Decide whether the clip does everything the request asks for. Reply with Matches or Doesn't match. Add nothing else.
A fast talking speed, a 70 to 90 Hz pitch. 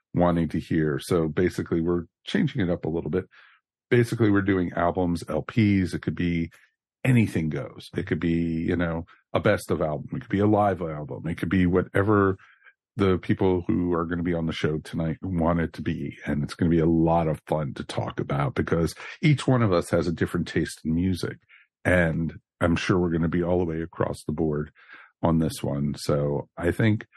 Matches